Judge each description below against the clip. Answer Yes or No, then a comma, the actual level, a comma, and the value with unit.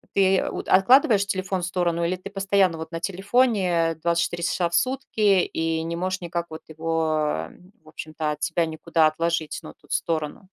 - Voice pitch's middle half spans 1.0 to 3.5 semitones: Yes, average, 2.8 semitones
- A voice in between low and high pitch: Yes, medium, 170 Hz